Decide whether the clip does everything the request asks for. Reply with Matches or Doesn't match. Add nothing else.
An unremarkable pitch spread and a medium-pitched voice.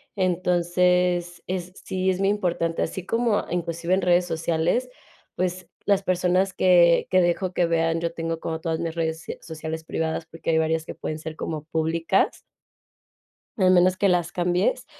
Doesn't match